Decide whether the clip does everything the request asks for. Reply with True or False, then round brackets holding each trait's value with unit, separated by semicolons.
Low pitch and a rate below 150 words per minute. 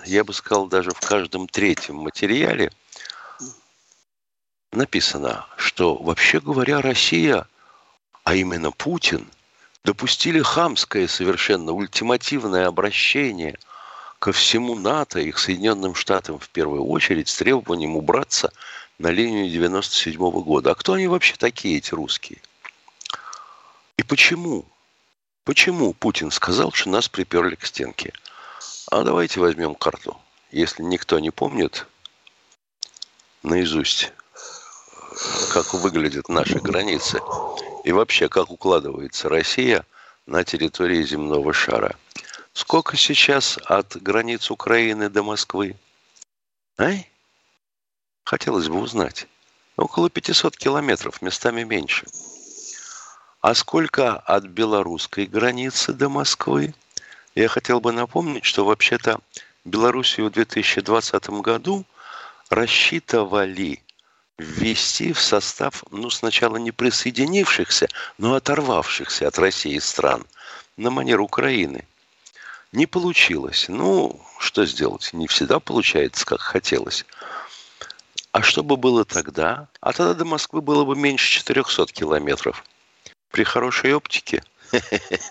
True (115 Hz; 110 wpm)